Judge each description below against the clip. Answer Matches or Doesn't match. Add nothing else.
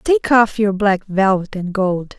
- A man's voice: Doesn't match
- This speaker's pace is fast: Doesn't match